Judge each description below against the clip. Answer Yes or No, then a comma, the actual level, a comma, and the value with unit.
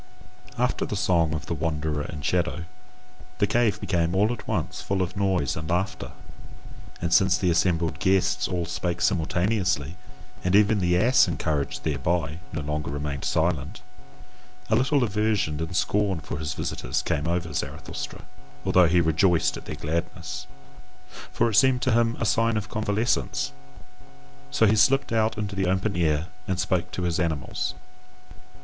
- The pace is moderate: Yes, average, 160 wpm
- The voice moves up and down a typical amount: Yes, average, 4.1 semitones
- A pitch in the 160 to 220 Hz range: No, very low, 90 Hz